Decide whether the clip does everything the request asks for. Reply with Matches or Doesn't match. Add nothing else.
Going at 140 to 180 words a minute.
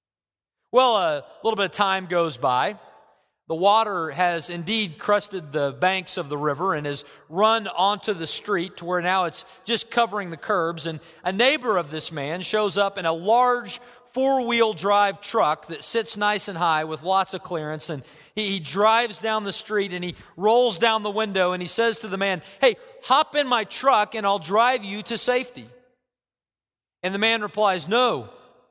Doesn't match